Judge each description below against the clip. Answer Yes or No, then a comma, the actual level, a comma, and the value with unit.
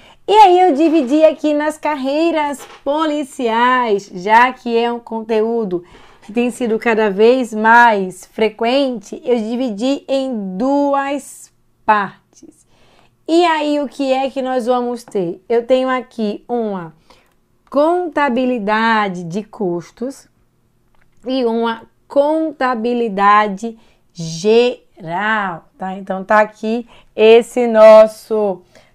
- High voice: Yes, high, 235 Hz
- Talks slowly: Yes, slow, 105 wpm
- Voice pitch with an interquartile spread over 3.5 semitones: Yes, average, 4.1 semitones